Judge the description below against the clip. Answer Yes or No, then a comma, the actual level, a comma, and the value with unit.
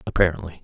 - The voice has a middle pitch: No, very low, 80 Hz